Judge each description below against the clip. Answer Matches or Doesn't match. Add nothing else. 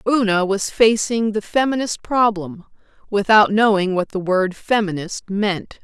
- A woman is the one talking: Matches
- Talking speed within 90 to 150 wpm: Matches